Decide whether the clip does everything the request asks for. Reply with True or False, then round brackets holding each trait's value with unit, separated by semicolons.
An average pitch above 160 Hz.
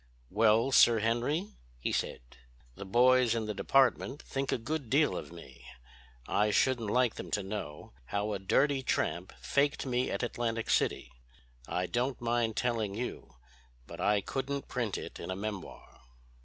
False (115 Hz)